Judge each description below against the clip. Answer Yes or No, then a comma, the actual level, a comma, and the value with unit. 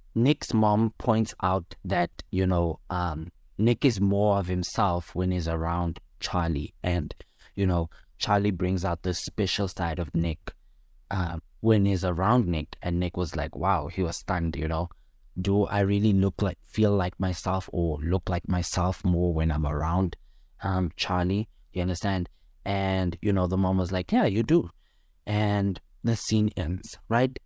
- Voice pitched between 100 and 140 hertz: No, very low, 90 Hz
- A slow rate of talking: No, average, 170 wpm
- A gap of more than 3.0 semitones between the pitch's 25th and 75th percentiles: No, average, 2.7 semitones